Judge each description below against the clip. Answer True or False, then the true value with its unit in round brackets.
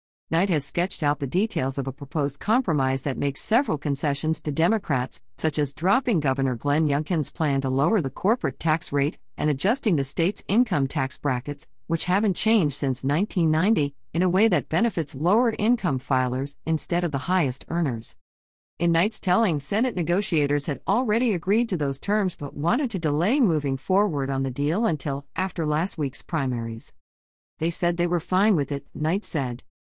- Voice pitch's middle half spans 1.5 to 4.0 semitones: False (5.3 semitones)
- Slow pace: False (175 wpm)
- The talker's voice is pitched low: False (155 Hz)